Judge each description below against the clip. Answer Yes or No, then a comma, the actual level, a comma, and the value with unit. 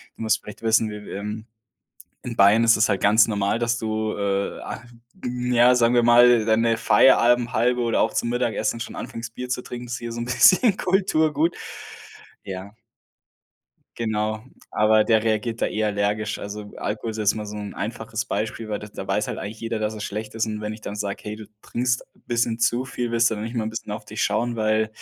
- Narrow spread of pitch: Yes, narrow, 2.0 semitones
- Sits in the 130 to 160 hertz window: No, low, 110 Hz